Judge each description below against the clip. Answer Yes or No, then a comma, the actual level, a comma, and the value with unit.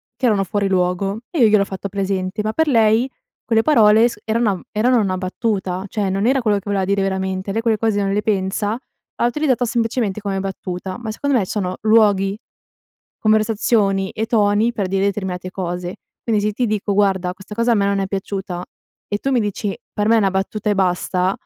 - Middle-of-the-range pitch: No, high, 205 Hz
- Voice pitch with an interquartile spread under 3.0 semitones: Yes, narrow, 2.5 semitones